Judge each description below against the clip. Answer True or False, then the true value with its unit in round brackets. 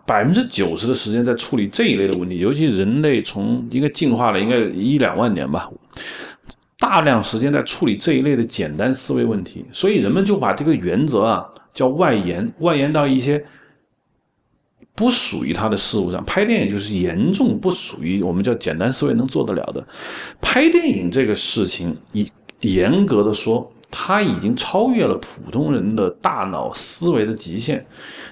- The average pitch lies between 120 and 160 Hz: True (140 Hz)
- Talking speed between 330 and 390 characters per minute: False (275 characters per minute)